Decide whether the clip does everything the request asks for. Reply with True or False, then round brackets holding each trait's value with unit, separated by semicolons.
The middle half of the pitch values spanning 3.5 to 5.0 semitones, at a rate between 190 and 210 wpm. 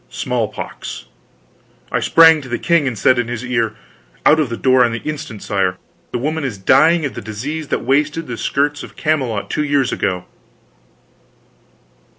False (4.6 semitones; 170 wpm)